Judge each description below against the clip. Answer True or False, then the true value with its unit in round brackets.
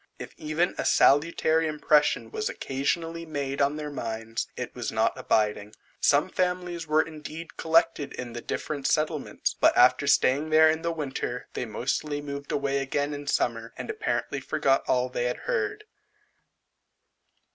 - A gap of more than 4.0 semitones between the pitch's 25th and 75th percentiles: False (3.4 semitones)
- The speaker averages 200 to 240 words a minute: False (150 wpm)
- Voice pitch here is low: False (150 Hz)